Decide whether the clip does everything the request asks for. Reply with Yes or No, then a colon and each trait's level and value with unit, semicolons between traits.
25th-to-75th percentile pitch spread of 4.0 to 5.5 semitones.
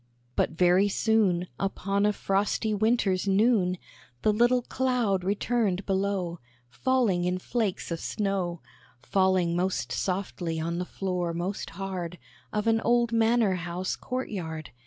No: average, 3.5 semitones